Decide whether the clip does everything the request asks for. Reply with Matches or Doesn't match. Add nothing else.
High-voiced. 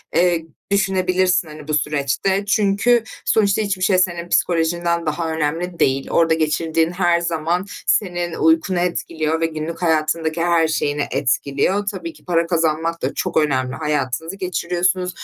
Doesn't match